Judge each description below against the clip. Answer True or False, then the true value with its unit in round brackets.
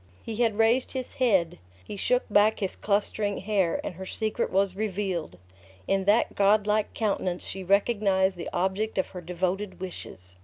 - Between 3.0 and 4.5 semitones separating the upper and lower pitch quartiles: False (2.5 semitones)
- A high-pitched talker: True (200 Hz)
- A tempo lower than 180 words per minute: True (165 wpm)